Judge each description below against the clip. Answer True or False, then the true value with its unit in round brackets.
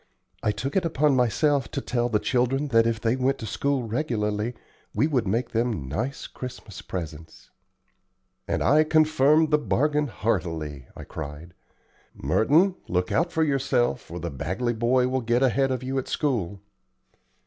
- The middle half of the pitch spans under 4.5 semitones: False (4.9 semitones)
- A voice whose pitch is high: False (125 Hz)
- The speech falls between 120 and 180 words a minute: True (160 wpm)